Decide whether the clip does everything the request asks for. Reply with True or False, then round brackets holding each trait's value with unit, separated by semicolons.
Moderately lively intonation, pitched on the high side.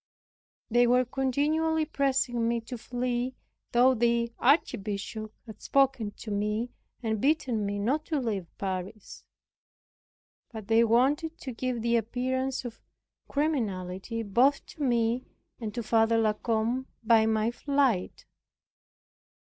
True (3.1 semitones; 235 Hz)